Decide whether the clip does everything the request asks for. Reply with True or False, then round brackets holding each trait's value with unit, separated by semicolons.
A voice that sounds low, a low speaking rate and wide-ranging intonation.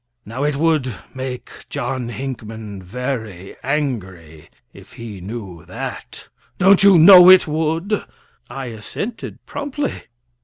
True (130 Hz; 115 wpm; 6.8 semitones)